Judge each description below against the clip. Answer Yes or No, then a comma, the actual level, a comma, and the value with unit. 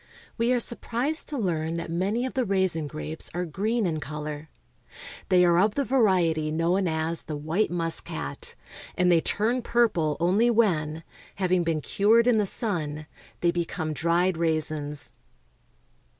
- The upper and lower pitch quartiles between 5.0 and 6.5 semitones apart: Yes, average, 5.3 semitones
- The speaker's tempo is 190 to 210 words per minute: No, average, 160 wpm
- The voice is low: No, medium, 175 Hz